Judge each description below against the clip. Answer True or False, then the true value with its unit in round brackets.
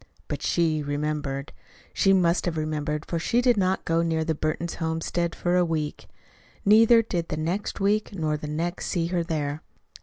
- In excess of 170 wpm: True (180 wpm)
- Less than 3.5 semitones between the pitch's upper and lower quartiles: True (2.8 semitones)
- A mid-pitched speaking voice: True (165 Hz)